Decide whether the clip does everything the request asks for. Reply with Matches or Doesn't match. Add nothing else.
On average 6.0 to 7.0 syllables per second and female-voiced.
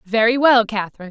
Matches